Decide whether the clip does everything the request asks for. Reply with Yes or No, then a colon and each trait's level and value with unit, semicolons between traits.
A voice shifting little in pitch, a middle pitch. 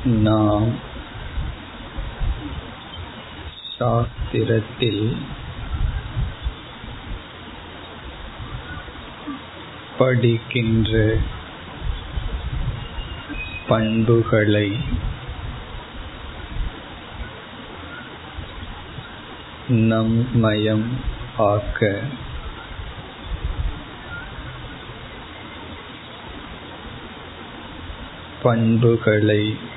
No: narrow, 2.0 semitones; low, 110 Hz